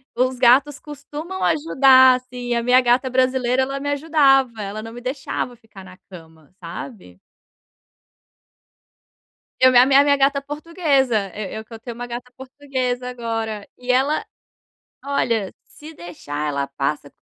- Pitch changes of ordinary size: Yes, average, 3.8 semitones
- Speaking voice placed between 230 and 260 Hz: Yes, very high, 250 Hz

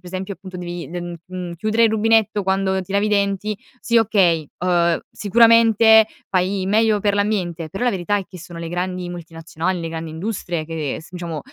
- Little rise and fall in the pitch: No, average, 3.3 semitones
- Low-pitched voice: No, medium, 185 Hz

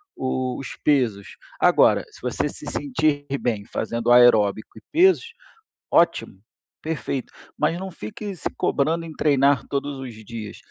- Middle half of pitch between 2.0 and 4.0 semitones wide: No, average, 4.9 semitones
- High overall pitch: No, low, 135 Hz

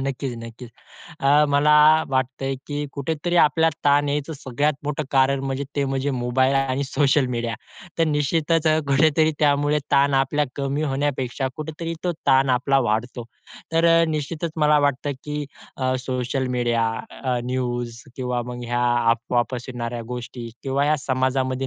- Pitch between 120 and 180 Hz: Yes, low, 135 Hz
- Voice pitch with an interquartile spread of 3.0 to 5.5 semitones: No, narrow, 2.6 semitones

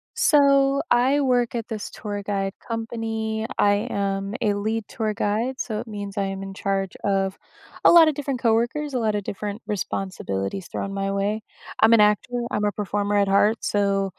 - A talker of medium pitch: No, high, 210 Hz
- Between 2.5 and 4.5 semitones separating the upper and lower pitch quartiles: Yes, average, 2.8 semitones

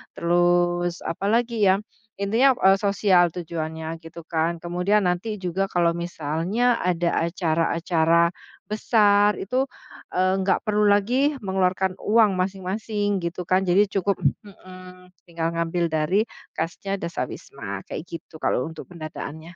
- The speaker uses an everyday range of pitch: Yes, average, 3.2 semitones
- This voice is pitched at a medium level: Yes, medium, 180 Hz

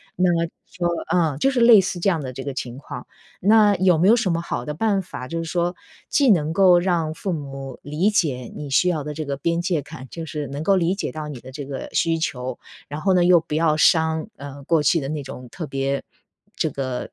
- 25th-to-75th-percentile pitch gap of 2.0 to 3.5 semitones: No, average, 4.3 semitones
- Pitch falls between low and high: Yes, medium, 160 Hz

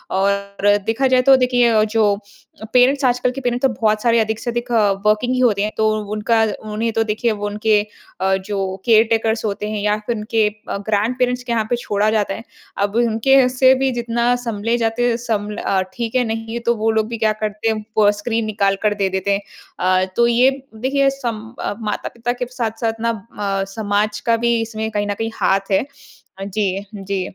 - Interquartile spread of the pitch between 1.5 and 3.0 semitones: Yes, narrow, 2.4 semitones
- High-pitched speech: Yes, high, 220 Hz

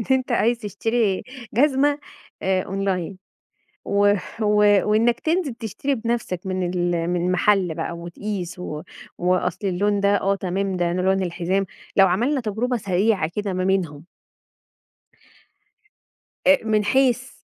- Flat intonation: No, average, 3.8 semitones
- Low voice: No, high, 195 Hz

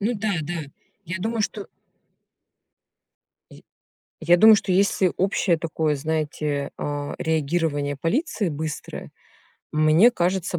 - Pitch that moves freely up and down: No, average, 4.3 semitones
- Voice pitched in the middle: Yes, medium, 165 Hz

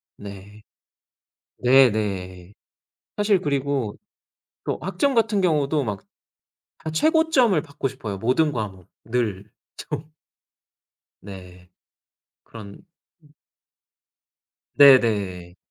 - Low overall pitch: Yes, low, 125 Hz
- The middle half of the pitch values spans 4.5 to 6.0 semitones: No, wide, 7.4 semitones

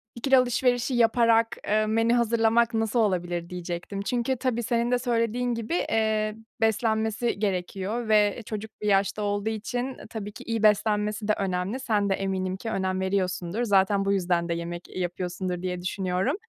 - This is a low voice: No, high, 215 Hz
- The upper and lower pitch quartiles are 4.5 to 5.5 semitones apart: No, average, 3.5 semitones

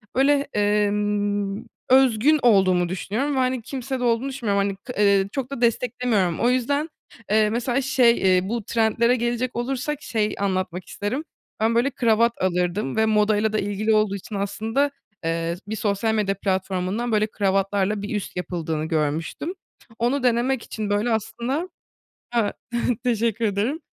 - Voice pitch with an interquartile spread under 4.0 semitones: Yes, average, 3.5 semitones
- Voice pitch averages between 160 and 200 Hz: No, high, 220 Hz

